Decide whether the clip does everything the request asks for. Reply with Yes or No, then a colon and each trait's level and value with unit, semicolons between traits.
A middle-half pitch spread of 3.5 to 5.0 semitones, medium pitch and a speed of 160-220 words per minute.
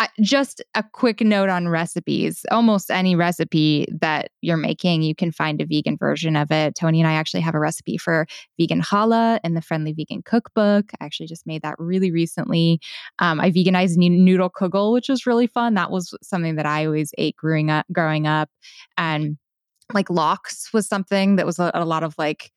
Yes: average, 4.2 semitones; medium, 175 Hz; average, 200 wpm